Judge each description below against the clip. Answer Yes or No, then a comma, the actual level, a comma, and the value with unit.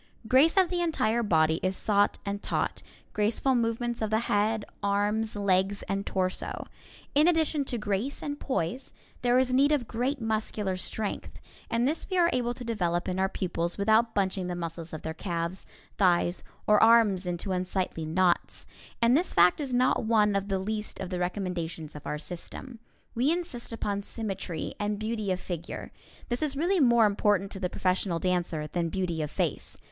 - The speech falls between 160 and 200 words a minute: Yes, average, 180 wpm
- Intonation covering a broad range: No, average, 4.6 semitones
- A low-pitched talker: No, high, 205 Hz